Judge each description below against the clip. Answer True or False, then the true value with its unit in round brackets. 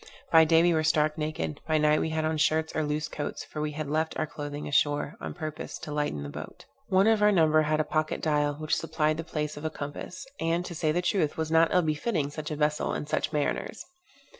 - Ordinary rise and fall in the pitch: False (1.3 semitones)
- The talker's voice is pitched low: False (155 Hz)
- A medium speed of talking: False (240 wpm)